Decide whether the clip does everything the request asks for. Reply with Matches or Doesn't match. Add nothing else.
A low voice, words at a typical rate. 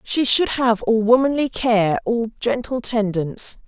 Doesn't match